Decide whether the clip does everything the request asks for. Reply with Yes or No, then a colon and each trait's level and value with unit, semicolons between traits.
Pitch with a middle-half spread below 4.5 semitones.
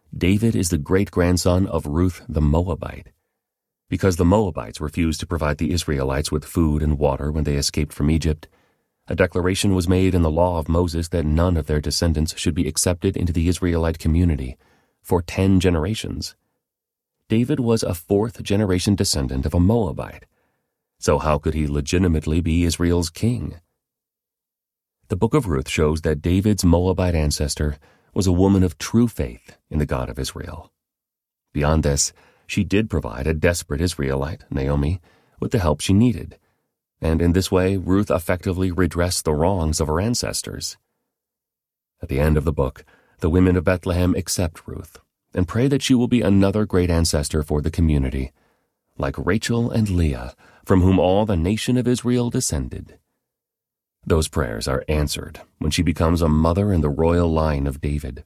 Yes: average, 3.7 semitones